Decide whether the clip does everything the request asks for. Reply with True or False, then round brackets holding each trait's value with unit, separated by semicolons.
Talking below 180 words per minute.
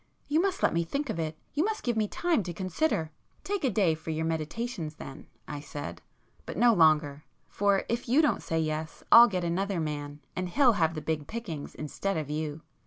False (200 wpm)